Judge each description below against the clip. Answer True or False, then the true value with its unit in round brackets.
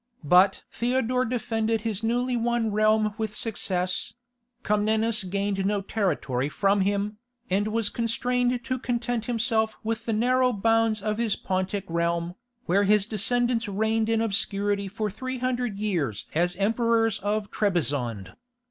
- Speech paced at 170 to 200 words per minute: False (140 wpm)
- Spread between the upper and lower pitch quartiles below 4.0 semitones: True (2.7 semitones)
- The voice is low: False (215 Hz)